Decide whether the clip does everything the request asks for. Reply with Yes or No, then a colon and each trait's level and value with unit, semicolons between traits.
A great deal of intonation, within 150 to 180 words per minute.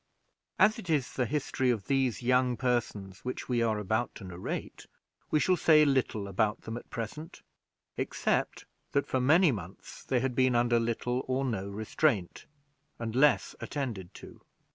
No: average, 3.6 semitones; average, 165 wpm